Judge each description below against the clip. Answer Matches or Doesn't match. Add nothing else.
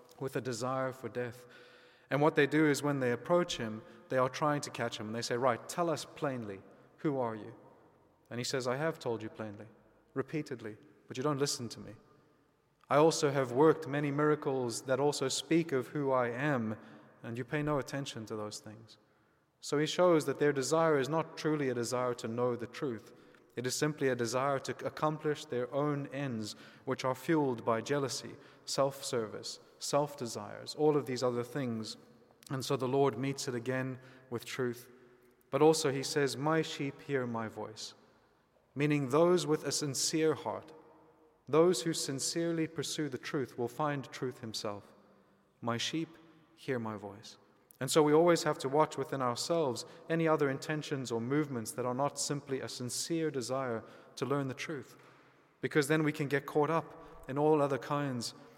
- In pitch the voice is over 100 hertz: Matches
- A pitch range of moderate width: Matches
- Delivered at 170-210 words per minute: Matches